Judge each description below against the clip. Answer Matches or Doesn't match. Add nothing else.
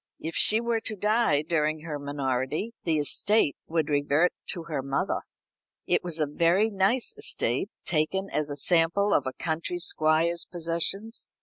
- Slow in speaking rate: Doesn't match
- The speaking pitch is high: Doesn't match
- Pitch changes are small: Doesn't match